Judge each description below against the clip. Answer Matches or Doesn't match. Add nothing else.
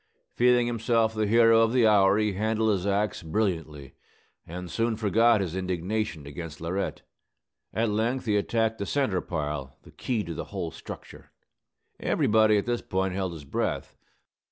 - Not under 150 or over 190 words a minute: Matches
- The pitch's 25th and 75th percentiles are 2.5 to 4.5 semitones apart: Matches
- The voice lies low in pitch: Matches